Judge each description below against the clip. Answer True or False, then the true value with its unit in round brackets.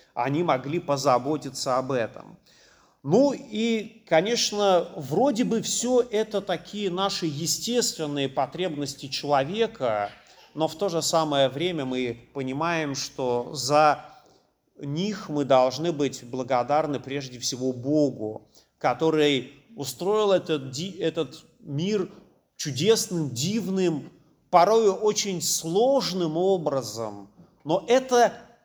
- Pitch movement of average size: False (6.0 semitones)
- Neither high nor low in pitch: True (160 Hz)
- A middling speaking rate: False (100 wpm)